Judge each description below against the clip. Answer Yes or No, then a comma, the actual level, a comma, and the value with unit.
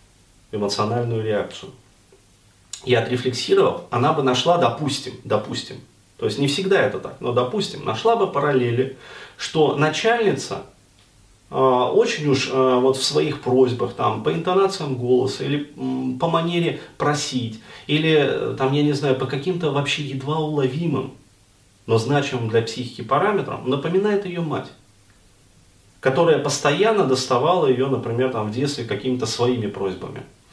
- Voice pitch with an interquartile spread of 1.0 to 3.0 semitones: No, average, 4.2 semitones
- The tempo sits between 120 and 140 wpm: Yes, average, 135 wpm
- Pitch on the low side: Yes, low, 130 Hz